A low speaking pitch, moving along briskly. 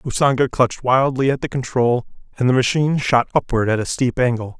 No: low, 125 Hz; average, 195 wpm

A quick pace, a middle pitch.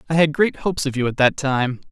Yes: fast, 280 wpm; medium, 145 Hz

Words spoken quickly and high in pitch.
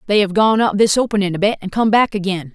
Yes: fast, 285 wpm; high, 205 Hz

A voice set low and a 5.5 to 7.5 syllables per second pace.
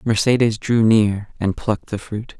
No: low, 110 Hz; 4.6 syllables/s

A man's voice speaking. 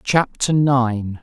Yes: male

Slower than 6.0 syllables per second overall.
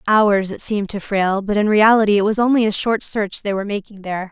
No: 6.3 syllables/s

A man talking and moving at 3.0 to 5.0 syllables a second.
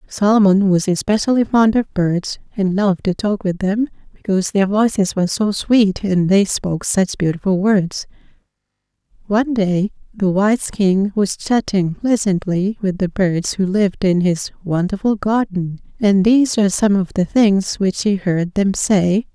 No: female; 4.5 syllables/s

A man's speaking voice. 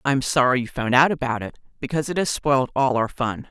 No: female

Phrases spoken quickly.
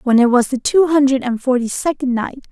Yes: fast, 240 wpm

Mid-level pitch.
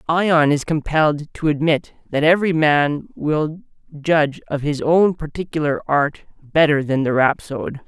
Yes: medium, 150 Hz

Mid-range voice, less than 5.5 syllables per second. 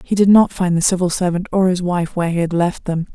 No: medium, 180 Hz; 6.1 syllables/s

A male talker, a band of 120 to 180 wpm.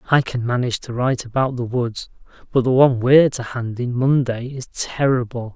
No: male; average, 195 wpm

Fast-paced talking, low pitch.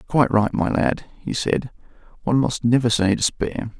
No: average, 175 wpm; low, 115 Hz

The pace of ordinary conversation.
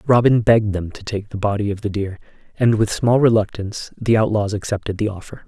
No: fast, 210 wpm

